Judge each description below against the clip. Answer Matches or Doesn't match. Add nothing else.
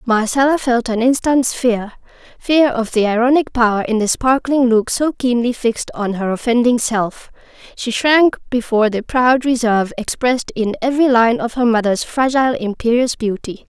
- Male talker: Doesn't match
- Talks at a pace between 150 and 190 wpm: Matches